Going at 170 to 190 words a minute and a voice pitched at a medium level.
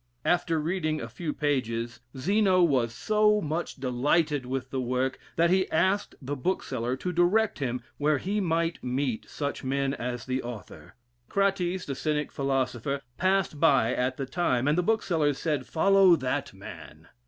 No: average, 160 wpm; medium, 145 Hz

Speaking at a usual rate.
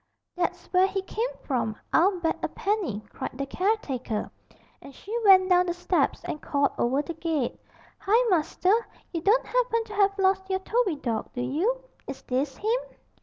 Yes: average, 175 wpm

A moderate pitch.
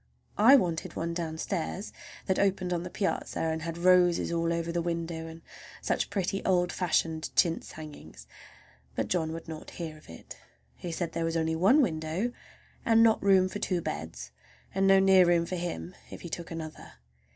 Yes: medium, 170 Hz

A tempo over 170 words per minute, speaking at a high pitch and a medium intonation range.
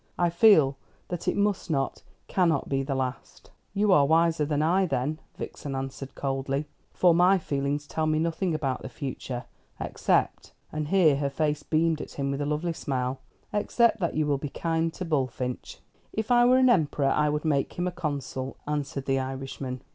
No: average, 185 wpm; medium, 150 Hz; average, 3.7 semitones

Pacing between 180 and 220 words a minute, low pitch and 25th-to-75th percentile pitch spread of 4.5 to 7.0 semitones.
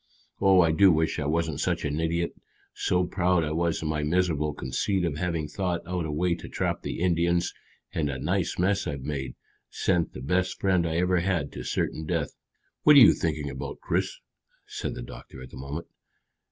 No: average, 200 wpm; very low, 85 Hz; average, 3.3 semitones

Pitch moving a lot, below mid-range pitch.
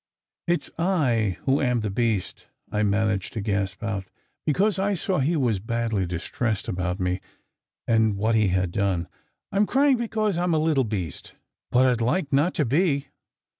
Yes: wide, 8.1 semitones; low, 115 Hz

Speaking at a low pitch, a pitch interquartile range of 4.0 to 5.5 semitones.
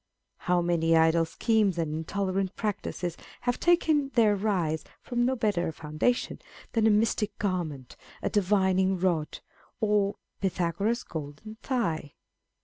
No: high, 190 Hz; average, 4.8 semitones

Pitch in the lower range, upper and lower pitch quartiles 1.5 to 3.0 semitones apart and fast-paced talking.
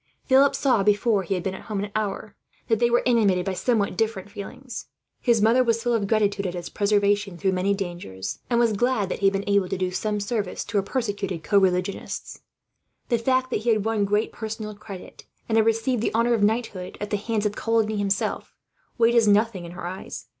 No: high, 210 Hz; narrow, 2.6 semitones; fast, 220 wpm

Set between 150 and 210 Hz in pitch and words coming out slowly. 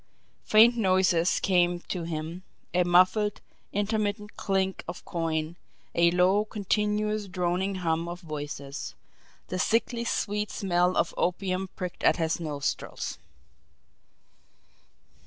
Yes: medium, 185 Hz; slow, 110 wpm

